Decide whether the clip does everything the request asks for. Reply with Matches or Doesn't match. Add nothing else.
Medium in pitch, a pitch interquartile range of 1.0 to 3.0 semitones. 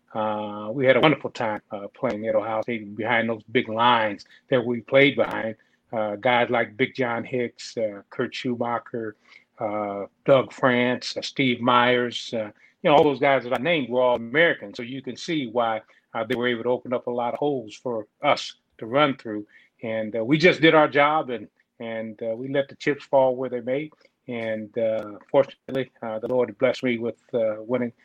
Doesn't match